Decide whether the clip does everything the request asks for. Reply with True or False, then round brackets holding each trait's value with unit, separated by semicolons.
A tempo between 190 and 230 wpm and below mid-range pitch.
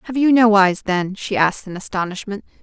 False (205 wpm; 205 Hz)